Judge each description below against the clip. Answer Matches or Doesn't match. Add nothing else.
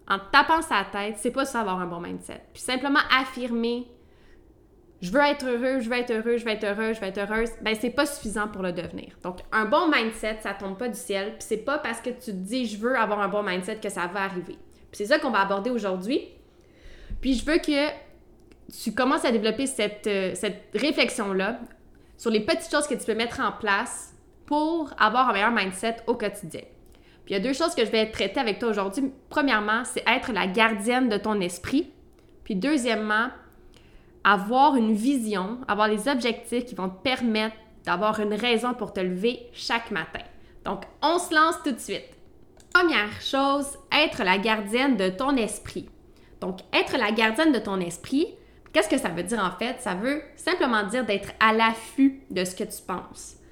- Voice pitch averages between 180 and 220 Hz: Doesn't match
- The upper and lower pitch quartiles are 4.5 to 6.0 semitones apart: Matches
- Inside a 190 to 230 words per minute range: Matches